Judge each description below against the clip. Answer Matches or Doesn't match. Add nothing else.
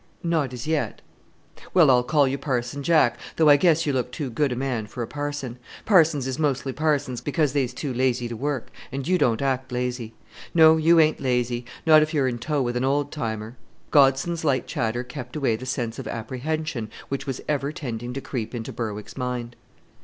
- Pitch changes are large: Doesn't match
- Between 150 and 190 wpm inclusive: Doesn't match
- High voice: Doesn't match